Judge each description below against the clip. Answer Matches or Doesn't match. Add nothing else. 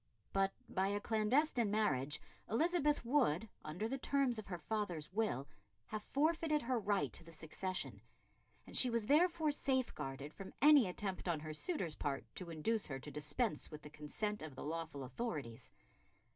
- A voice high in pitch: Matches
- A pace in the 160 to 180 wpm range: Matches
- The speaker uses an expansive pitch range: Matches